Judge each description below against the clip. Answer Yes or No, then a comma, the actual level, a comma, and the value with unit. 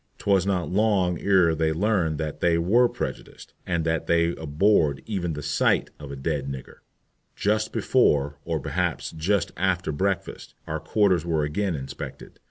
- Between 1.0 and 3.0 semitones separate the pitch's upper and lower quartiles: No, average, 4.1 semitones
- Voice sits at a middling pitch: No, very low, 85 Hz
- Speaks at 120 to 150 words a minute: No, average, 165 wpm